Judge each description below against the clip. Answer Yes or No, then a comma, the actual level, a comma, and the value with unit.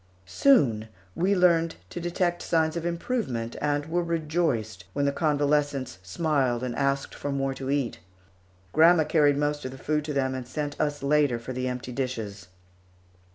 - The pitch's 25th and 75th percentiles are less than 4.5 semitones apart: Yes, average, 3.9 semitones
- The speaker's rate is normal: Yes, average, 165 wpm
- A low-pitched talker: No, medium, 145 Hz